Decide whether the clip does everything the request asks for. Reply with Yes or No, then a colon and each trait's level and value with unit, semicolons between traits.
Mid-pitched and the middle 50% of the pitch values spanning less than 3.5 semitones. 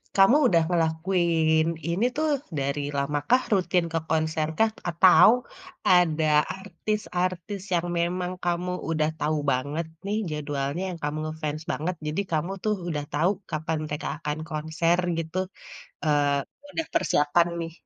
Yes: medium, 165 Hz; average, 2.9 semitones